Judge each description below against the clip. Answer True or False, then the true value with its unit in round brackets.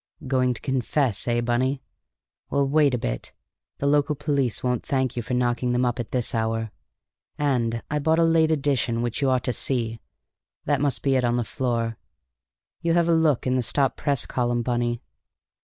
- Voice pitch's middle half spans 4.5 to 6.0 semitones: False (2.9 semitones)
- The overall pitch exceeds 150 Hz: False (125 Hz)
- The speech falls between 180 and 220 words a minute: True (190 wpm)